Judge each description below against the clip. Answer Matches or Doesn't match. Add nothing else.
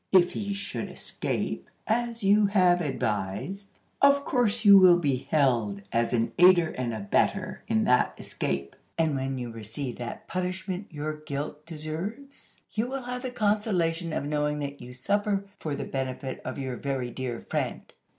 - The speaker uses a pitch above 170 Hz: Doesn't match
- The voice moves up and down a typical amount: Doesn't match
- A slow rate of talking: Doesn't match